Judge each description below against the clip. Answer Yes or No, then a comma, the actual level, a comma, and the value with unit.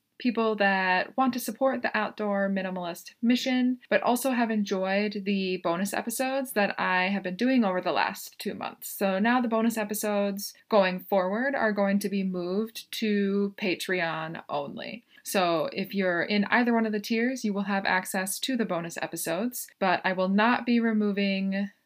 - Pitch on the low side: No, high, 205 Hz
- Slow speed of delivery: No, average, 175 wpm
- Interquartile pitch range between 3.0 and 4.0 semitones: Yes, average, 3.6 semitones